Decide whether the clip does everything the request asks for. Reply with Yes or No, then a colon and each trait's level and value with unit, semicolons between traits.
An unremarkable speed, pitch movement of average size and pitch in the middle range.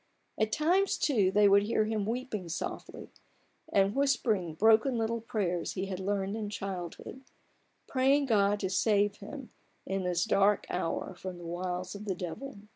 No: average, 165 wpm; average, 3.3 semitones; high, 205 Hz